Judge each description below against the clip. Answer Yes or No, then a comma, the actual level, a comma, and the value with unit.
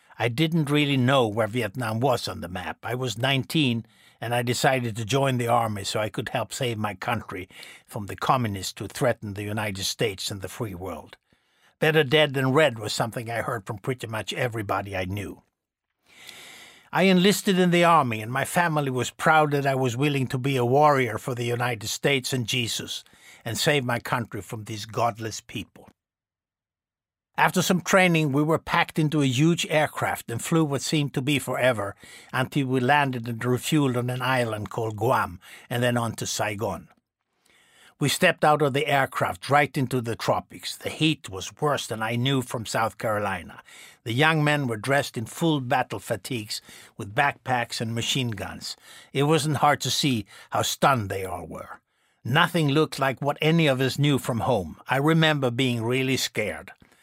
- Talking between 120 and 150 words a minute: No, average, 185 wpm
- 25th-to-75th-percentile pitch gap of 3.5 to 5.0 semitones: Yes, average, 4.3 semitones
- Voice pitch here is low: Yes, low, 130 Hz